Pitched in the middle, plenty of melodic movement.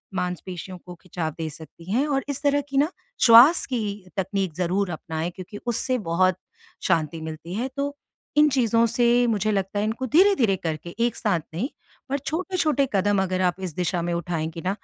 No: high, 195 Hz; wide, 6.7 semitones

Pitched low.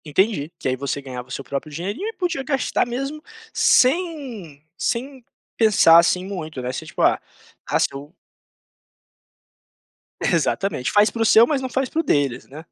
No: high, 200 Hz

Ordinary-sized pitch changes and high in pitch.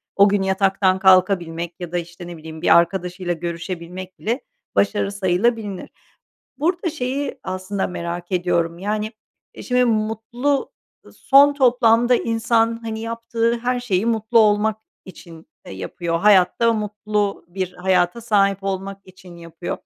Yes: average, 4.3 semitones; high, 195 Hz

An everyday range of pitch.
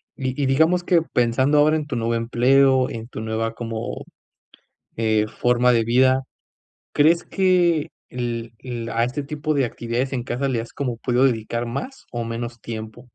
Yes: average, 3.1 semitones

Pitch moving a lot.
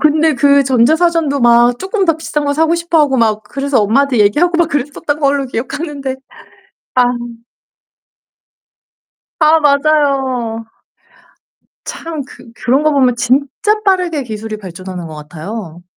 No: average, 4.8 semitones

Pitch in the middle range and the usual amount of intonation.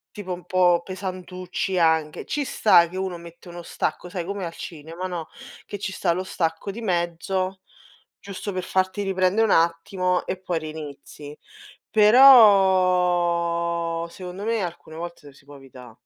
No: medium, 180 Hz; narrow, 2.1 semitones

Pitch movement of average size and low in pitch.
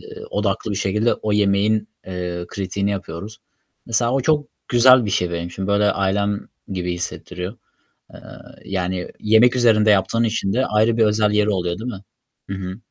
Yes: average, 3.1 semitones; low, 105 Hz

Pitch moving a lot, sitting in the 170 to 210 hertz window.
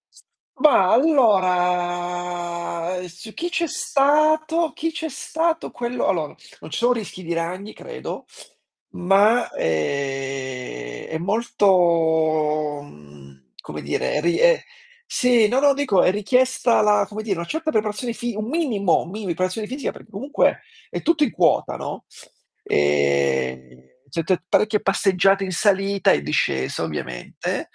Yes: wide, 7.3 semitones; high, 190 Hz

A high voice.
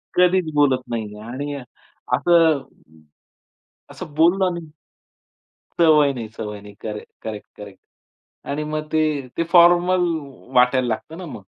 No: medium, 145 Hz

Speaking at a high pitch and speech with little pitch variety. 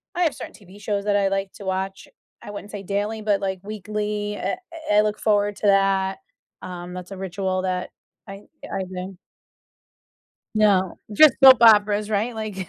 Yes: high, 200 Hz; narrow, 1.7 semitones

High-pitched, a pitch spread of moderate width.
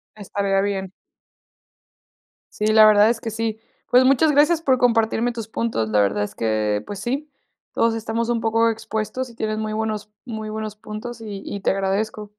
No: high, 220 Hz; narrow, 2.1 semitones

